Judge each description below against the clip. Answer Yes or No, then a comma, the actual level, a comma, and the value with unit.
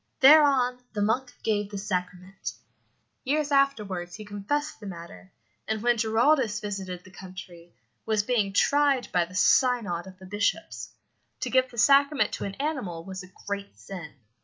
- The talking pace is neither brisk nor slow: Yes, average, 160 wpm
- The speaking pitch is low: No, high, 205 Hz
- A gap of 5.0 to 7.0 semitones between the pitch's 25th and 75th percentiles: Yes, wide, 5.5 semitones